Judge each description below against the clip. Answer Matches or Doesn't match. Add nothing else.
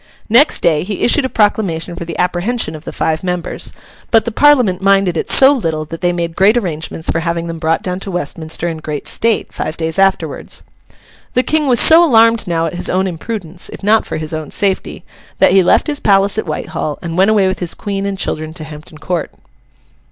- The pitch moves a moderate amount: Matches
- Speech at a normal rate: Doesn't match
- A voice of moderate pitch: Matches